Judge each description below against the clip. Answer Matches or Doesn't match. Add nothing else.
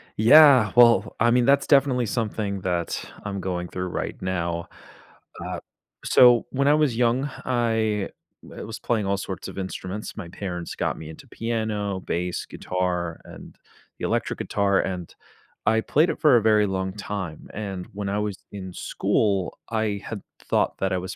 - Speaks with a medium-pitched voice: Doesn't match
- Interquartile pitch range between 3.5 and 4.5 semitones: Matches